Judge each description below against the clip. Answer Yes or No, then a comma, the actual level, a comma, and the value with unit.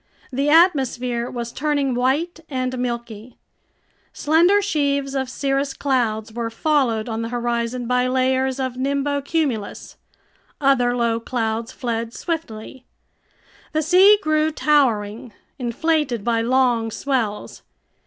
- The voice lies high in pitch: Yes, very high, 255 Hz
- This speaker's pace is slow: Yes, slow, 115 wpm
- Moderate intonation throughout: Yes, average, 3.4 semitones